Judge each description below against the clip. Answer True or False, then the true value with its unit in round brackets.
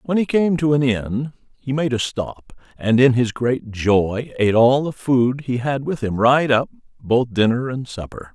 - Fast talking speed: True (210 wpm)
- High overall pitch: False (125 Hz)